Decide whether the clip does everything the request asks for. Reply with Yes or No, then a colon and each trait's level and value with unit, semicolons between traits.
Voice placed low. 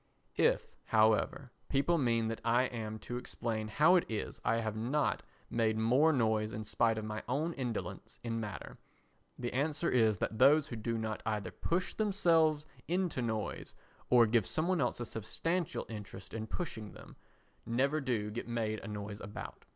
Yes: low, 115 Hz